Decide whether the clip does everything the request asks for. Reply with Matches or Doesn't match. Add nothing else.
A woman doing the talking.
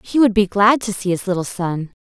Matches